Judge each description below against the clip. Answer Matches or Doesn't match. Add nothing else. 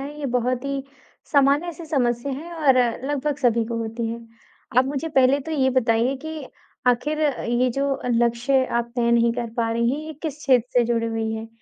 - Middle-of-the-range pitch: Doesn't match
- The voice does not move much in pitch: Doesn't match